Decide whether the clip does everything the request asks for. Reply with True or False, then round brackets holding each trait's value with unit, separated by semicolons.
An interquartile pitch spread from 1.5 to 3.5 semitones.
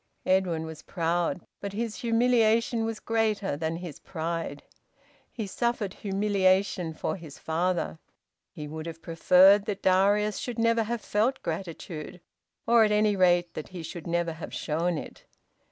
False (4.3 semitones)